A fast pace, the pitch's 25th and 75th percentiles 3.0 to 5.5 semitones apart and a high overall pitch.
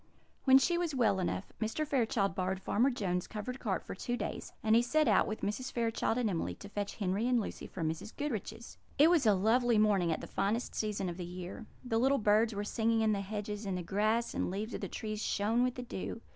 Yes: fast, 235 wpm; average, 3.5 semitones; high, 215 Hz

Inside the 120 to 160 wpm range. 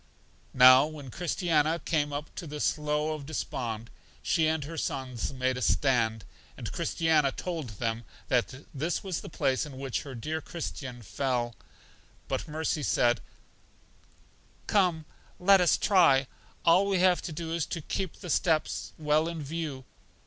Yes: average, 155 wpm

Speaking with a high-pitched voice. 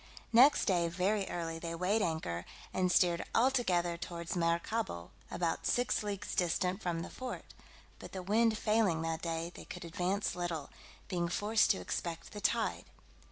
No: medium, 180 Hz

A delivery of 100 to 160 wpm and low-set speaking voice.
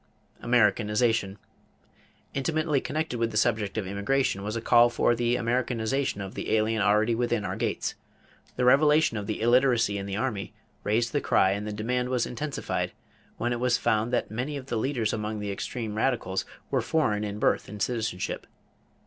No: average, 175 wpm; low, 115 Hz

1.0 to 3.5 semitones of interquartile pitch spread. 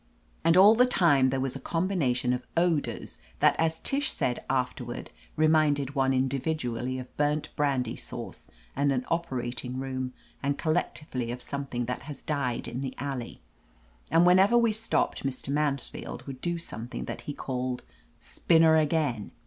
No: average, 4.1 semitones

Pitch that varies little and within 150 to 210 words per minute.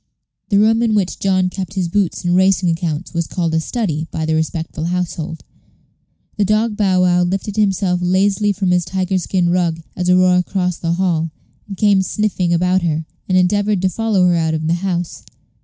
Yes: narrow, 2.3 semitones; average, 190 wpm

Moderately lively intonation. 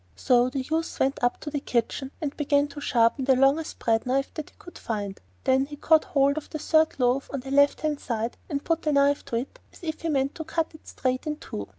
Yes: average, 3.2 semitones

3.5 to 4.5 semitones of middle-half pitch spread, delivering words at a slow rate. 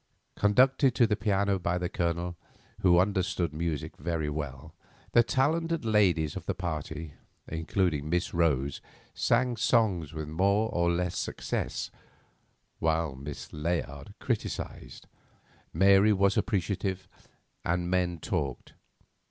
Yes: average, 4.2 semitones; slow, 120 wpm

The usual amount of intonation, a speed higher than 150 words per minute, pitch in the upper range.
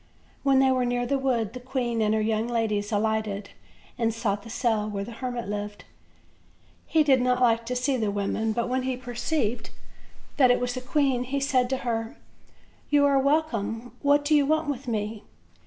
Yes: average, 3.2 semitones; average, 195 wpm; high, 245 Hz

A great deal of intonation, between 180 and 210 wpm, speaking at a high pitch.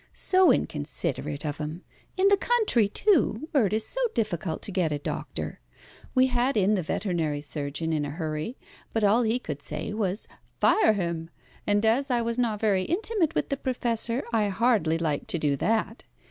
Yes: wide, 7.1 semitones; average, 185 wpm; high, 210 Hz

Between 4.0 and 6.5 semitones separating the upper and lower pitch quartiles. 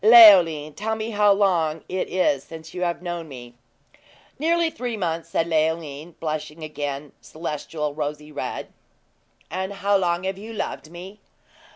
Yes: average, 4.6 semitones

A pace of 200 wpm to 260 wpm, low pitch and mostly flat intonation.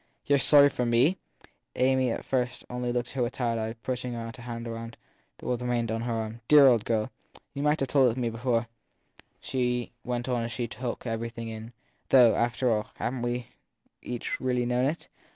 Yes: fast, 205 wpm; low, 120 Hz; narrow, 1.6 semitones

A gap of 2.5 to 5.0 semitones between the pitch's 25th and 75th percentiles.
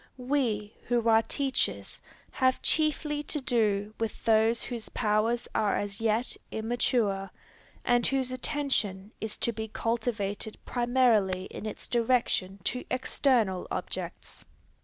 Yes: average, 3.1 semitones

